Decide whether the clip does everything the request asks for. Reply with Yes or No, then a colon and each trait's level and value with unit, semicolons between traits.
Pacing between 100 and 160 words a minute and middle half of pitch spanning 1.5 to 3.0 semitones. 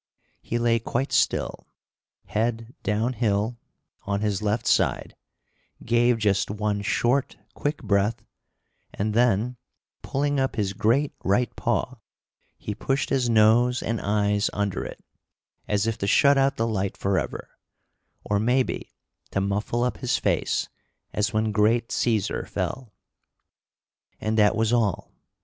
Yes: slow, 135 wpm; average, 2.7 semitones